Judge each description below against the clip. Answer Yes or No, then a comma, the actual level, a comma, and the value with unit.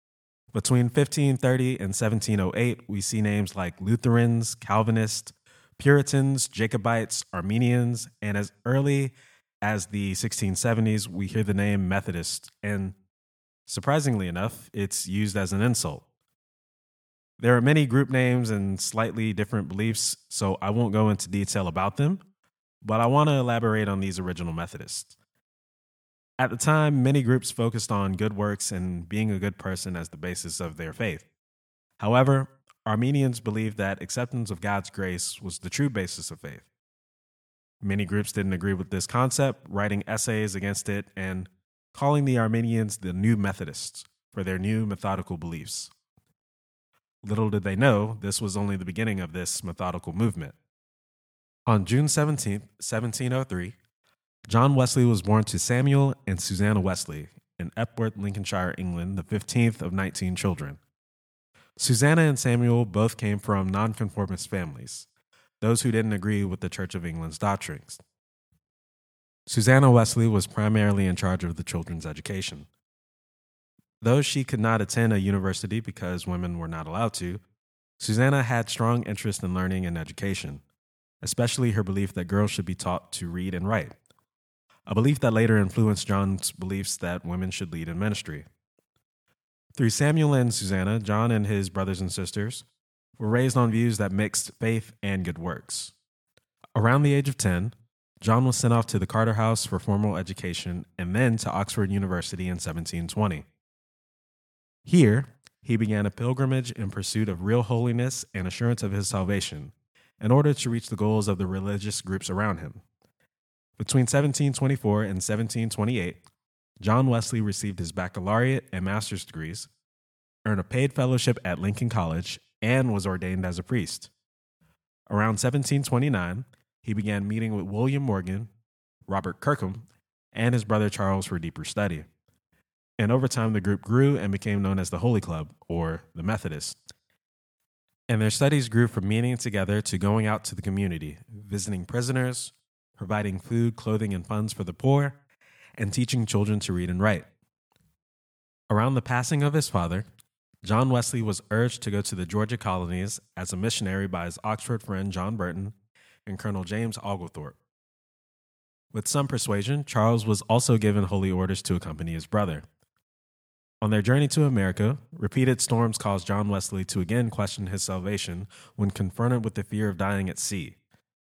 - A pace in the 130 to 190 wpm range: Yes, average, 160 wpm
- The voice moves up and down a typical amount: Yes, average, 3.8 semitones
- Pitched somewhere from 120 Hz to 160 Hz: No, low, 105 Hz